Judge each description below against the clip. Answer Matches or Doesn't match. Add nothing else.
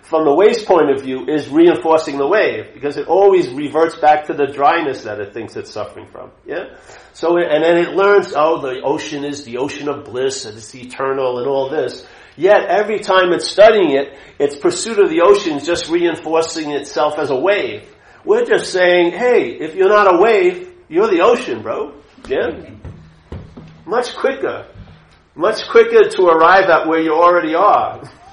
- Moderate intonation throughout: Doesn't match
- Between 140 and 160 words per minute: Doesn't match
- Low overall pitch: Doesn't match